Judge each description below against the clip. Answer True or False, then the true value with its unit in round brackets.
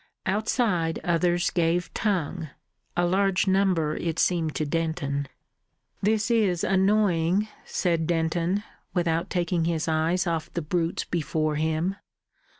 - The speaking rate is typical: False (120 wpm)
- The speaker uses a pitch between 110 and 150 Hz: False (170 Hz)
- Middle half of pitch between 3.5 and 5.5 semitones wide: False (2.7 semitones)